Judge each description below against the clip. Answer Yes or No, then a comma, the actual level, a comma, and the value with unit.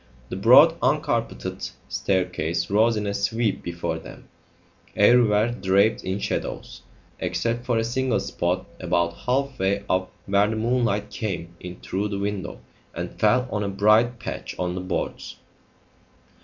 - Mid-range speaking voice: No, low, 100 Hz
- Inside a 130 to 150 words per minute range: Yes, average, 145 wpm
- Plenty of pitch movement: No, average, 3.7 semitones